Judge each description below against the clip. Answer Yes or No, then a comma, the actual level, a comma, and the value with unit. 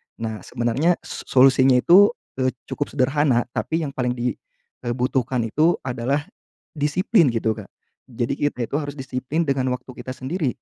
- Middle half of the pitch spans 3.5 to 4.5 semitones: No, average, 3.0 semitones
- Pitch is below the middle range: Yes, low, 130 Hz